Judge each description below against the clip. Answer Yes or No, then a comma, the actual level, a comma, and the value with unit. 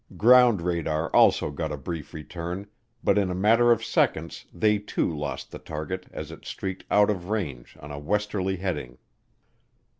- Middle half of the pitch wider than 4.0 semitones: Yes, average, 5.1 semitones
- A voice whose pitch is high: No, very low, 90 Hz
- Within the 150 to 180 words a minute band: Yes, average, 170 wpm